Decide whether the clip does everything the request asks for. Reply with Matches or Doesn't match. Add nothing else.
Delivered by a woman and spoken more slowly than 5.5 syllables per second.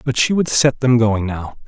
Doesn't match